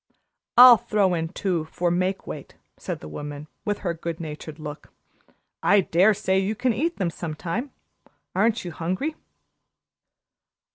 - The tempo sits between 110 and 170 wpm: Yes, average, 150 wpm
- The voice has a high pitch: No, medium, 180 Hz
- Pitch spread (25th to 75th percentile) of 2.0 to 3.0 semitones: No, average, 4.2 semitones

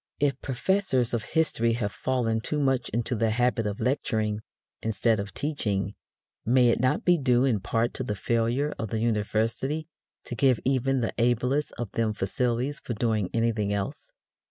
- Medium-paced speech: Yes, average, 170 wpm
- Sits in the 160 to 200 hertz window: No, low, 120 Hz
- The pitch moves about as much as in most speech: Yes, average, 3.0 semitones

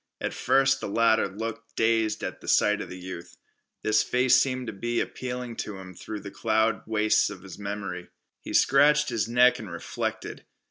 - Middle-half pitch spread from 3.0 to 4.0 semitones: Yes, average, 3.5 semitones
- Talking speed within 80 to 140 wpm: No, average, 185 wpm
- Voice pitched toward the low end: Yes, low, 110 Hz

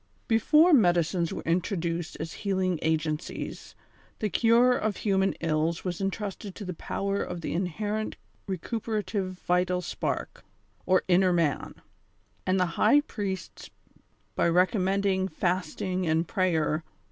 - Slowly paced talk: Yes, slow, 125 wpm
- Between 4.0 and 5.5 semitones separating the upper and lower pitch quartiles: No, average, 2.8 semitones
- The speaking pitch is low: No, medium, 185 Hz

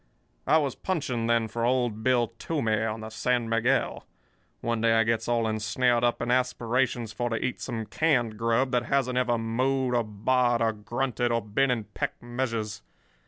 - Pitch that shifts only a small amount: Yes, narrow, 2.1 semitones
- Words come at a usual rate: Yes, average, 180 wpm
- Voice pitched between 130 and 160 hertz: No, low, 120 Hz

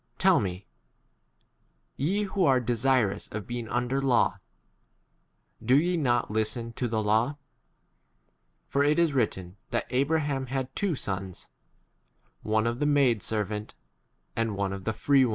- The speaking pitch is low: Yes, low, 120 Hz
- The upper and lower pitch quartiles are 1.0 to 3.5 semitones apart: No, average, 4.6 semitones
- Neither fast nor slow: Yes, average, 155 wpm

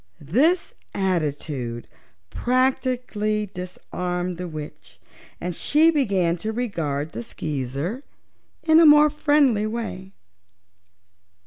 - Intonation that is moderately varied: No, wide, 7.5 semitones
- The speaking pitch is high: Yes, high, 195 Hz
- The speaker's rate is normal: No, slow, 95 wpm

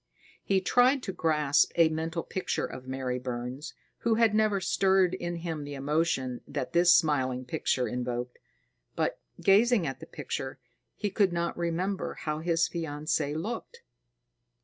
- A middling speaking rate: Yes, average, 150 wpm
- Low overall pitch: No, medium, 165 Hz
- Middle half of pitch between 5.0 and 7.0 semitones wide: Yes, wide, 5.6 semitones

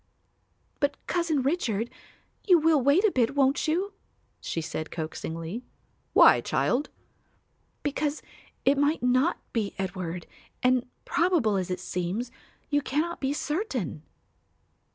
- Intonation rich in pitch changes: Yes, wide, 7.7 semitones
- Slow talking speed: Yes, slow, 120 wpm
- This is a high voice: Yes, very high, 265 Hz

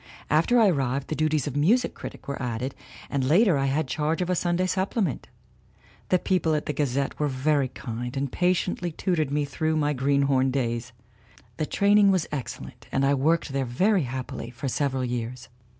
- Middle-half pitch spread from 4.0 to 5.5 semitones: Yes, average, 4.3 semitones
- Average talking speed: Yes, average, 185 wpm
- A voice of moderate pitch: Yes, medium, 145 Hz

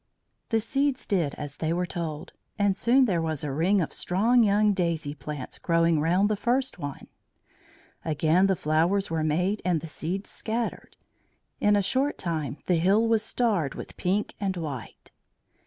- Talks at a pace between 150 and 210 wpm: Yes, average, 170 wpm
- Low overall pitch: No, medium, 180 Hz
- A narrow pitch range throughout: No, average, 4.7 semitones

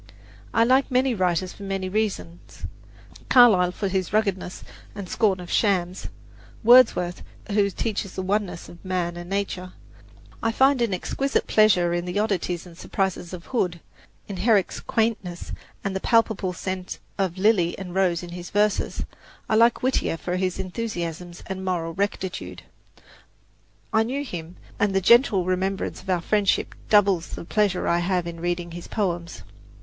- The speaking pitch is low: No, high, 190 Hz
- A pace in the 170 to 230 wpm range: No, average, 155 wpm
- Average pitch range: Yes, average, 3.1 semitones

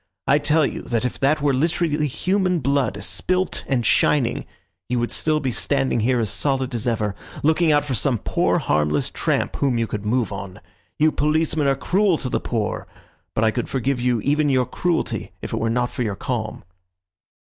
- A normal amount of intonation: Yes, average, 4.4 semitones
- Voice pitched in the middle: No, low, 130 Hz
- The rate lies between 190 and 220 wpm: Yes, average, 195 wpm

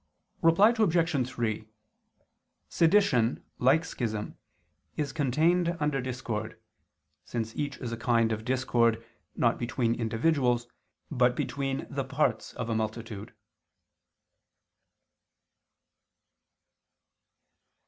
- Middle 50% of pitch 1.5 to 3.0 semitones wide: No, average, 4.3 semitones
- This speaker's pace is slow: Yes, slow, 90 wpm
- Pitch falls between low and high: No, low, 125 Hz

